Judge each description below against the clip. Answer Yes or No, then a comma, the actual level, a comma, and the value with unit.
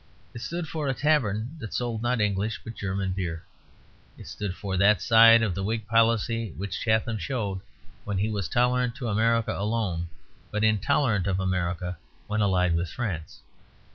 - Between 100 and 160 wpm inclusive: No, average, 170 wpm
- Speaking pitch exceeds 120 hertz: No, low, 105 Hz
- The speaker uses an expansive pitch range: No, average, 3.3 semitones